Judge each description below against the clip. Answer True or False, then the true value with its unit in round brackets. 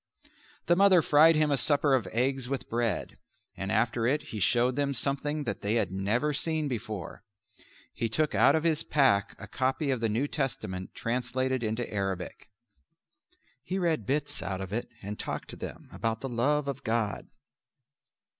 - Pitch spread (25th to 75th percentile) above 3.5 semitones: True (4.8 semitones)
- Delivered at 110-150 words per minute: False (175 wpm)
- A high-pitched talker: False (125 Hz)